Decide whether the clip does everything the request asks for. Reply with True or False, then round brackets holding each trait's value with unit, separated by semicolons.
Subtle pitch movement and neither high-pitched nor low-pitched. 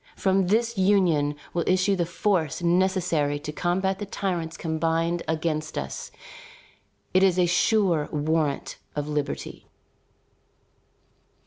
False (3.4 semitones; 170 Hz)